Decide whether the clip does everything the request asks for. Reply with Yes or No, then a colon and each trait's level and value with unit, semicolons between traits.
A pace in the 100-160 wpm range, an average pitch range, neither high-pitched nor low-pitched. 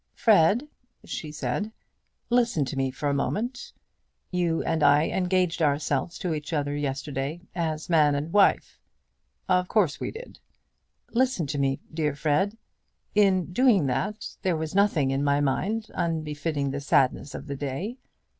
Yes: average, 150 wpm; average, 4.9 semitones; medium, 160 Hz